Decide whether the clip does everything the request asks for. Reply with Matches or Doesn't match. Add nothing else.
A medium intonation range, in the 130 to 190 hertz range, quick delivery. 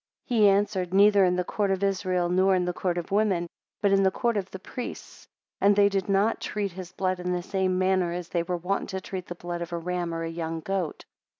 Doesn't match